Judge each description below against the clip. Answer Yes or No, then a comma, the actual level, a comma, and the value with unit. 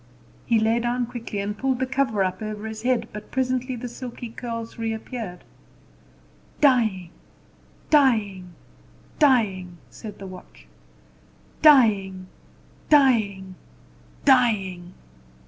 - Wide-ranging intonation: No, average, 4.2 semitones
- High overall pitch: Yes, high, 225 Hz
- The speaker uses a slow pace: Yes, slow, 105 wpm